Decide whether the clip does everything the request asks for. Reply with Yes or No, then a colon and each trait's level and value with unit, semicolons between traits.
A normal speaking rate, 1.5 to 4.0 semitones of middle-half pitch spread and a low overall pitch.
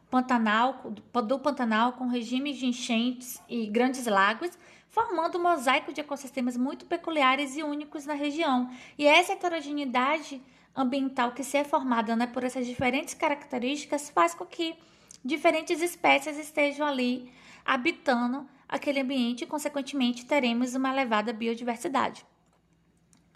No: average, 130 wpm; average, 3.3 semitones; very high, 265 Hz